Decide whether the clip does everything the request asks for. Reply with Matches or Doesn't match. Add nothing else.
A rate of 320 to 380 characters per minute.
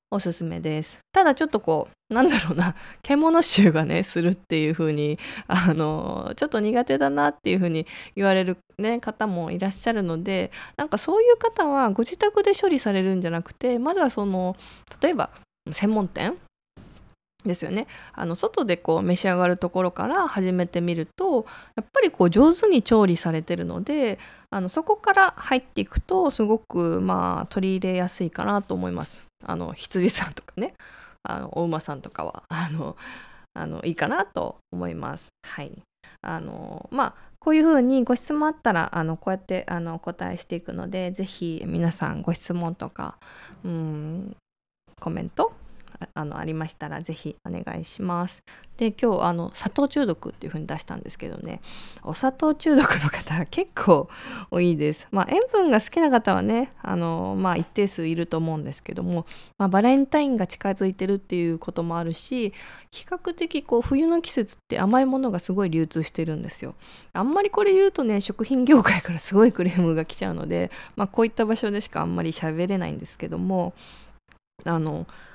Matches